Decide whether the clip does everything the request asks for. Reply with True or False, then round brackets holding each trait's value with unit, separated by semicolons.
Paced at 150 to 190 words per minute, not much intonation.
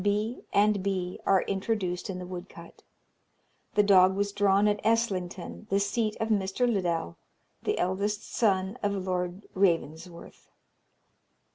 False (135 wpm; 2.2 semitones)